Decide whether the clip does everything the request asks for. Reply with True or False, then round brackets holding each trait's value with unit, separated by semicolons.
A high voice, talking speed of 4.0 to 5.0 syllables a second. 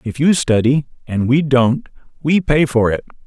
False (135 Hz; 4.5 syllables/s)